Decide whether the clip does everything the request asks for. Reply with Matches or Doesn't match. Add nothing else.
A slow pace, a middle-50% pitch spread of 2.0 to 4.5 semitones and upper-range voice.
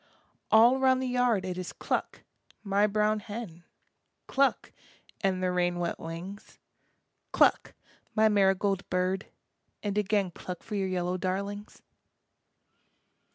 Matches